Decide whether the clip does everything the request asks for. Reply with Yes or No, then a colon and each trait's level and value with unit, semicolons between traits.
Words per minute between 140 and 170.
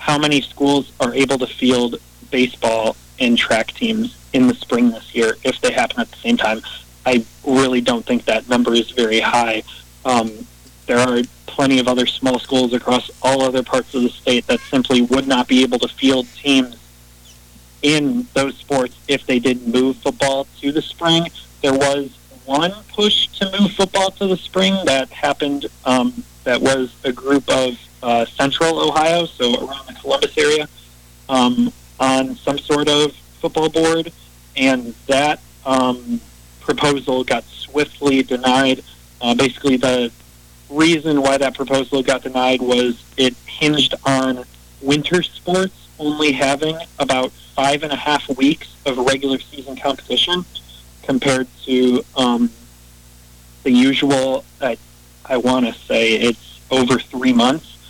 Yes: average, 155 wpm